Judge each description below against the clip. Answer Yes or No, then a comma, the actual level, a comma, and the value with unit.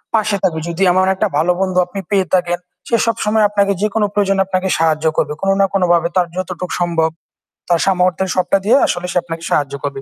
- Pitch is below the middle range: No, medium, 185 Hz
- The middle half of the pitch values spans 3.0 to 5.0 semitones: No, narrow, 2.5 semitones